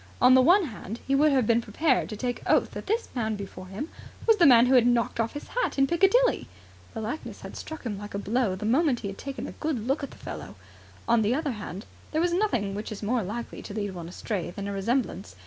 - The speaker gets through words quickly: Yes, fast, 250 wpm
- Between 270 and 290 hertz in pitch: No, high, 235 Hz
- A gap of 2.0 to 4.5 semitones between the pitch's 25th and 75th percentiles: No, wide, 5.5 semitones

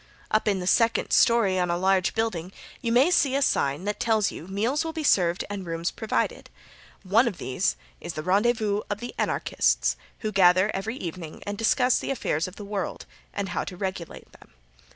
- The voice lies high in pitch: Yes, high, 200 Hz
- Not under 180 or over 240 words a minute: Yes, average, 195 wpm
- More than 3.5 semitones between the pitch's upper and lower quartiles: Yes, average, 3.9 semitones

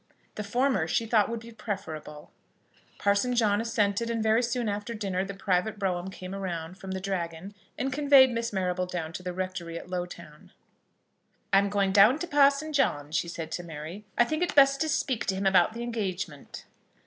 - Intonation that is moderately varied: Yes, average, 4.4 semitones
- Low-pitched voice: No, high, 200 Hz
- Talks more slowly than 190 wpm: No, average, 195 wpm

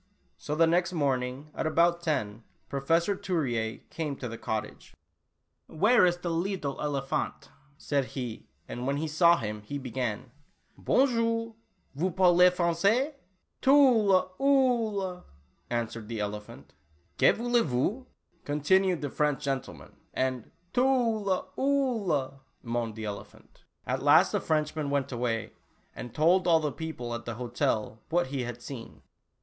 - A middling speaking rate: Yes, average, 145 wpm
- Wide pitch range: Yes, wide, 7.0 semitones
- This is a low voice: No, medium, 150 Hz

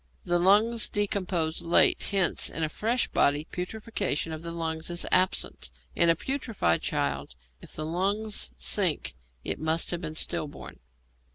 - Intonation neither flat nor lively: Yes, average, 4.2 semitones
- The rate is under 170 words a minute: Yes, average, 150 wpm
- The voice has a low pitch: No, medium, 175 Hz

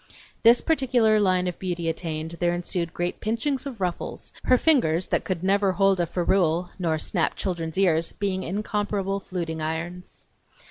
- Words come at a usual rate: Yes, average, 155 wpm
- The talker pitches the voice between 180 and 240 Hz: Yes, medium, 185 Hz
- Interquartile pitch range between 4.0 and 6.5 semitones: No, average, 3.3 semitones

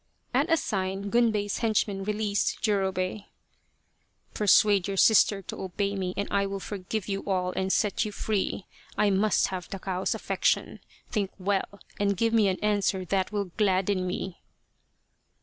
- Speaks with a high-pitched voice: Yes, high, 200 Hz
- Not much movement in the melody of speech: Yes, narrow, 1.8 semitones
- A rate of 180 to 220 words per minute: No, average, 160 wpm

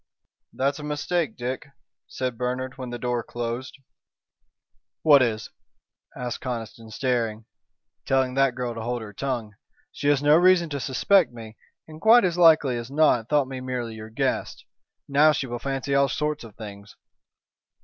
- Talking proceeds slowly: No, average, 160 wpm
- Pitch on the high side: No, low, 130 Hz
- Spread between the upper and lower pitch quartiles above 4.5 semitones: No, average, 3.6 semitones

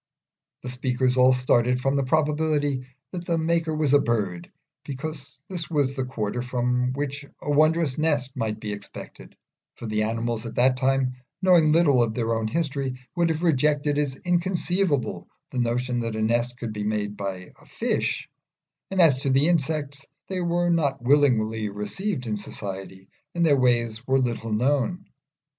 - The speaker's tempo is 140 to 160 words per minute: No, average, 170 wpm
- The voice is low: Yes, low, 130 Hz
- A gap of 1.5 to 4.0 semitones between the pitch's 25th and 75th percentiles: No, average, 4.6 semitones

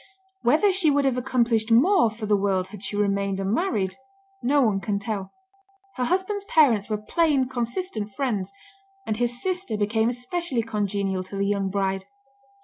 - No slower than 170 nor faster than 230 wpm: No, average, 160 wpm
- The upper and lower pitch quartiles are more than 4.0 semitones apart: Yes, average, 5.2 semitones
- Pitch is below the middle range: No, high, 225 Hz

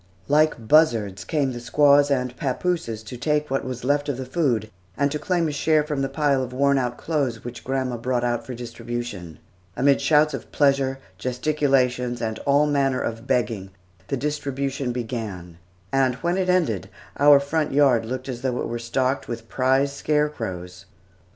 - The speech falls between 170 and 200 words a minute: Yes, average, 175 wpm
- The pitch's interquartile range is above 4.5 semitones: No, average, 3.3 semitones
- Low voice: Yes, low, 130 Hz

